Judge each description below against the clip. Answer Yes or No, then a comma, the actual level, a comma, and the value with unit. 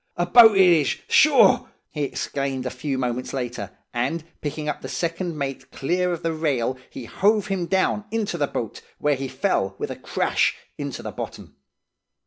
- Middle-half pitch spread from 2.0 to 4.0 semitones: No, average, 5.3 semitones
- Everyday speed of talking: Yes, average, 180 wpm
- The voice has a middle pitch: Yes, medium, 150 Hz